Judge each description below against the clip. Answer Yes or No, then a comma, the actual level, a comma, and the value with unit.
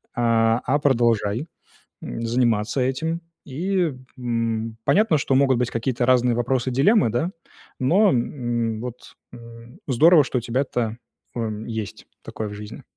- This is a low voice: Yes, low, 120 Hz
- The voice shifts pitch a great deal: No, average, 2.9 semitones